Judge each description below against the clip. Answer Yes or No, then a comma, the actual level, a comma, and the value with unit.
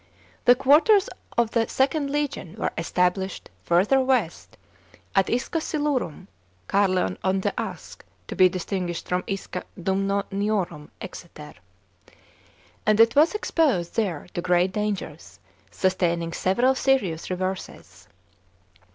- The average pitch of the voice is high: Yes, high, 195 Hz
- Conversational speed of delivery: No, slow, 115 wpm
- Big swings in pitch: Yes, wide, 5.7 semitones